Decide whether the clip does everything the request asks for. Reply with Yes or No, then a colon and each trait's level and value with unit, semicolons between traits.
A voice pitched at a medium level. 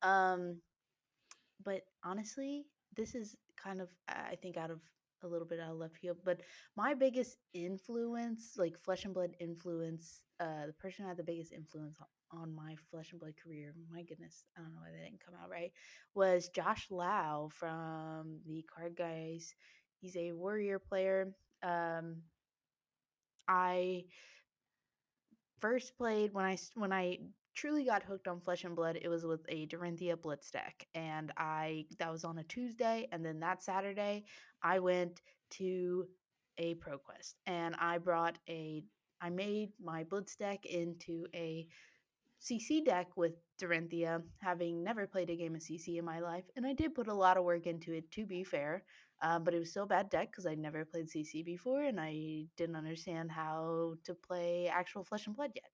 Yes: medium, 175 Hz